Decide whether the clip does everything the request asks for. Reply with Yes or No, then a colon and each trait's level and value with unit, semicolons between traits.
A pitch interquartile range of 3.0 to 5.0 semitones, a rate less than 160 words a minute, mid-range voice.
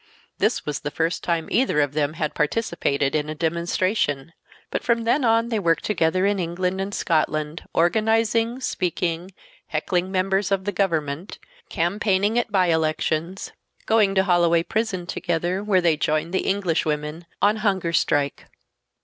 Yes: average, 3.9 semitones; average, 150 wpm; medium, 175 Hz